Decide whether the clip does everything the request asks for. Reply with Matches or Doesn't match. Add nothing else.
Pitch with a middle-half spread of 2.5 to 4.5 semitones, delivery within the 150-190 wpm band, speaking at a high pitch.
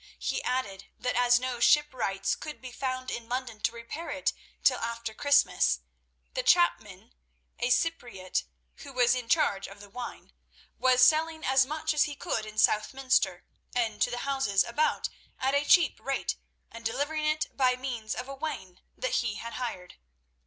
Matches